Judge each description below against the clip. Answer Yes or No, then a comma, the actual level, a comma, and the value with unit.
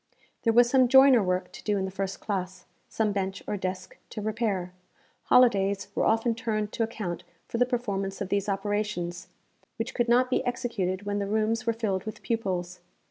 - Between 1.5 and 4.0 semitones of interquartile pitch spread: Yes, average, 3.2 semitones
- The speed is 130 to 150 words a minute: No, average, 190 wpm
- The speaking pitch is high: Yes, high, 210 Hz